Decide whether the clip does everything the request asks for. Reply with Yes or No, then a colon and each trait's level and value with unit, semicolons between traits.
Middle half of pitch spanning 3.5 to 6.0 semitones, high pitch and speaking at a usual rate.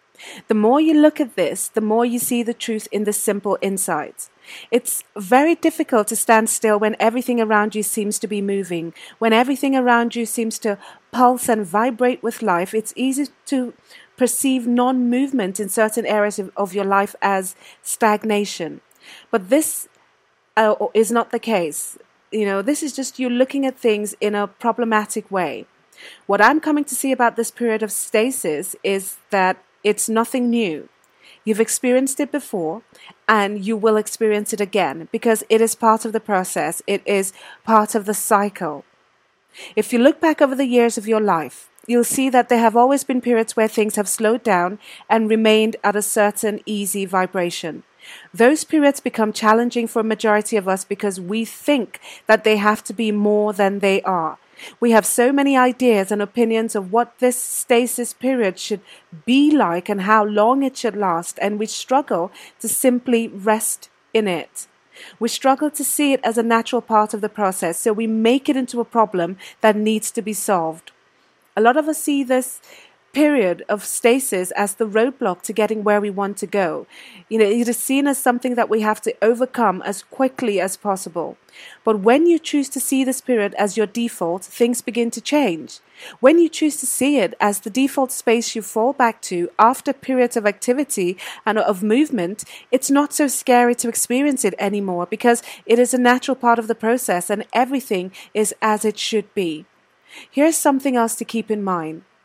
No: average, 3.1 semitones; high, 225 Hz; average, 185 wpm